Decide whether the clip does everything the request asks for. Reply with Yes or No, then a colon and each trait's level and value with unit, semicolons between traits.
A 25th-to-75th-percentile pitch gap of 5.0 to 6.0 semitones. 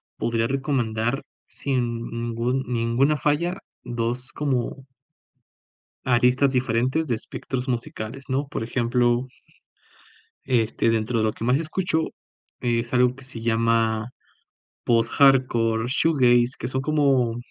No: narrow, 2.5 semitones